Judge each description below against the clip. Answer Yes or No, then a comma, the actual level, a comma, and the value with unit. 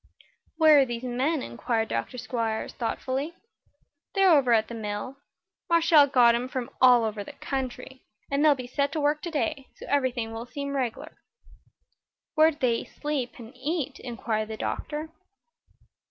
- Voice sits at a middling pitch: No, very high, 255 Hz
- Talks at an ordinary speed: Yes, average, 155 wpm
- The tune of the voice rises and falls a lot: No, average, 3.9 semitones